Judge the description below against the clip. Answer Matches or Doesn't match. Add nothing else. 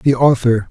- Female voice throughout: Doesn't match